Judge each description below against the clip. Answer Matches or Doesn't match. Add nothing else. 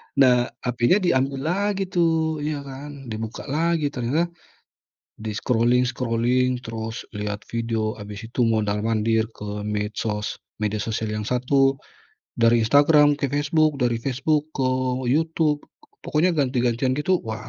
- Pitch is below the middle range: Matches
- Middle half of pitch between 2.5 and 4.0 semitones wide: Doesn't match